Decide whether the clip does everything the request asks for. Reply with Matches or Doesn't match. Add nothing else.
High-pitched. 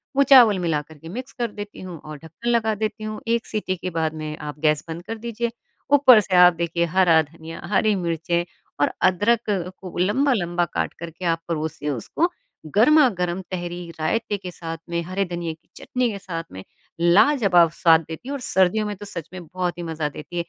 Doesn't match